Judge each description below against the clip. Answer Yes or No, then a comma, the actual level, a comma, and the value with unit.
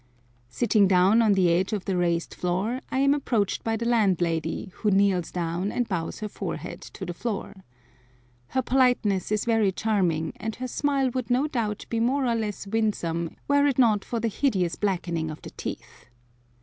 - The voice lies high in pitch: Yes, high, 210 Hz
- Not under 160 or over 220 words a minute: Yes, average, 185 wpm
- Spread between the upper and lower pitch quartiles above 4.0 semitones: Yes, average, 4.6 semitones